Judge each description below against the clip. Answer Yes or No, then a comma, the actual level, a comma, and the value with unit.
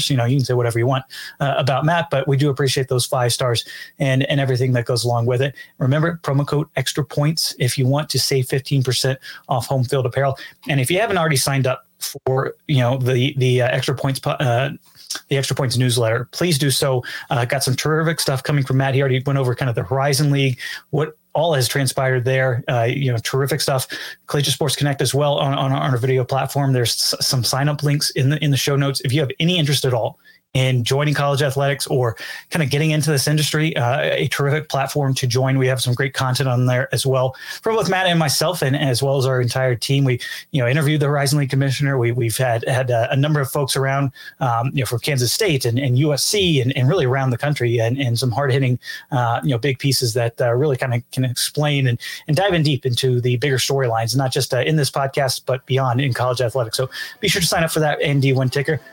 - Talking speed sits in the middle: No, fast, 240 wpm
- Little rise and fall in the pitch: Yes, narrow, 2.0 semitones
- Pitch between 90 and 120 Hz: No, low, 135 Hz